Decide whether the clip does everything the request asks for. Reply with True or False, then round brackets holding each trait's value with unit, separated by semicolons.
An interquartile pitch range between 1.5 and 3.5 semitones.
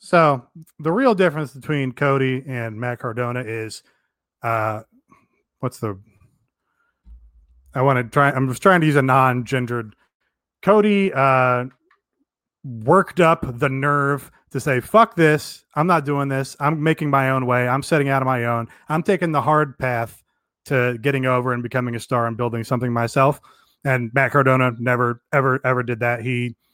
True (3.1 semitones)